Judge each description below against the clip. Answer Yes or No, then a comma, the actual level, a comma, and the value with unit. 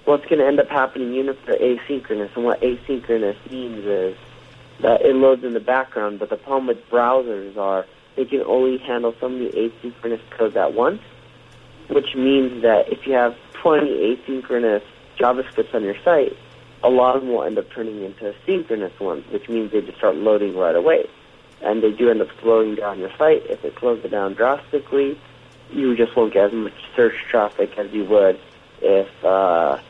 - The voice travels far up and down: No, average, 3.3 semitones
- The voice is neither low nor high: No, low, 125 Hz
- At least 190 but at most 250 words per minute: Yes, average, 195 wpm